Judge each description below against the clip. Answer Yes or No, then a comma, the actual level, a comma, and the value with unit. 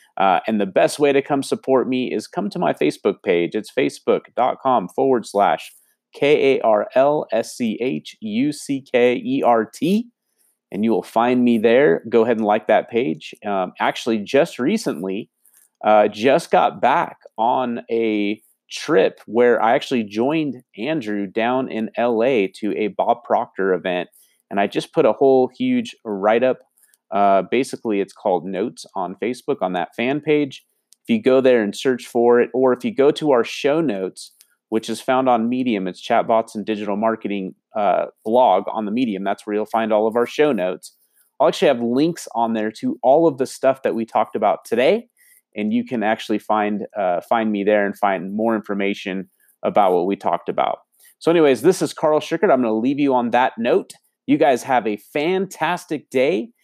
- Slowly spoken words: No, average, 195 wpm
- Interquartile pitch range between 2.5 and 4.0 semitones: No, average, 4.5 semitones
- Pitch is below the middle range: Yes, low, 120 Hz